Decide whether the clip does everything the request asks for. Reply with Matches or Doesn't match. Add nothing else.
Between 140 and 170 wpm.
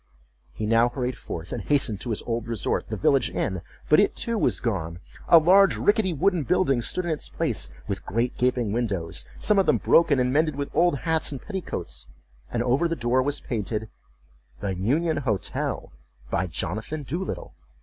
Doesn't match